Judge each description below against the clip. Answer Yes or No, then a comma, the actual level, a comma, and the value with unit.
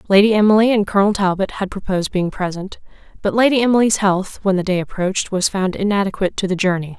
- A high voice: Yes, high, 195 Hz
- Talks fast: No, average, 195 wpm